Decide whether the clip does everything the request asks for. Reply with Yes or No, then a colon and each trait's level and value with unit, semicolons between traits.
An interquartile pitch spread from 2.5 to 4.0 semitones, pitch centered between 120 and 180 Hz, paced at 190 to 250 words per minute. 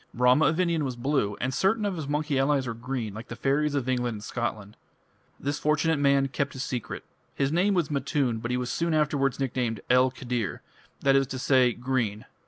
Yes: average, 3.3 semitones; low, 135 Hz; average, 200 wpm